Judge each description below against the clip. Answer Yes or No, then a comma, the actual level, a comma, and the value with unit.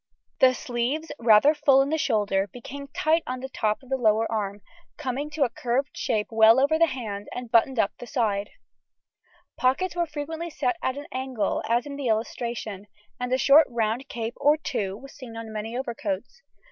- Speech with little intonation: No, average, 4.2 semitones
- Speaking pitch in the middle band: No, very high, 250 Hz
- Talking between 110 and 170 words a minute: No, average, 180 wpm